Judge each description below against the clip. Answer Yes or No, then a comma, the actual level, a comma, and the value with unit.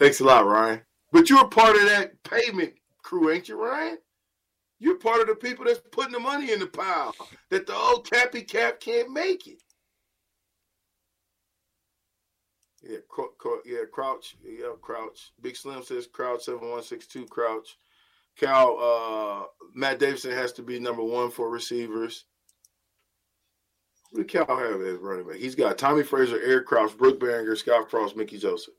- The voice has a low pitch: No, medium, 145 Hz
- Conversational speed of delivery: Yes, average, 165 wpm